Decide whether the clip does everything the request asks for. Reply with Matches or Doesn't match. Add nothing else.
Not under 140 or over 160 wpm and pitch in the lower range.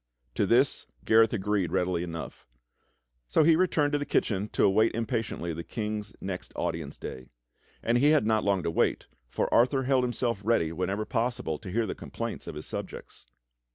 Doesn't match